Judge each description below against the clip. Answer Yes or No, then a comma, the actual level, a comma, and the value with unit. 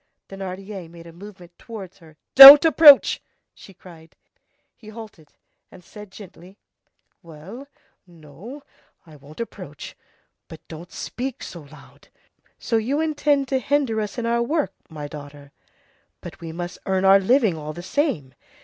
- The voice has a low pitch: No, high, 190 Hz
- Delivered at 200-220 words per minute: No, average, 145 wpm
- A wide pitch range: Yes, wide, 6.5 semitones